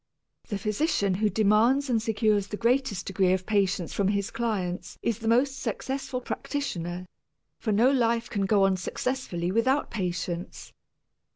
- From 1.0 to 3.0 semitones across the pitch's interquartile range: No, average, 3.9 semitones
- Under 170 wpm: Yes, average, 150 wpm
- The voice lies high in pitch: Yes, high, 215 Hz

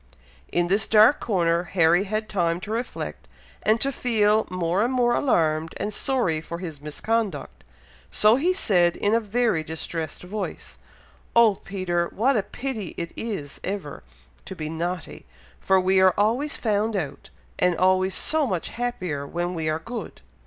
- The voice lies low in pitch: No, high, 190 Hz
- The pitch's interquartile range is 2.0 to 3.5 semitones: No, average, 4.7 semitones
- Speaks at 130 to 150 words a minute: No, average, 160 wpm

